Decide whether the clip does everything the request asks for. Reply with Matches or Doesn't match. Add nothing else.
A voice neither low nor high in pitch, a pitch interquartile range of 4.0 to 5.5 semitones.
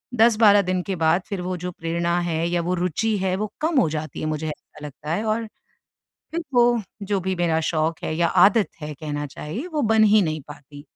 Matches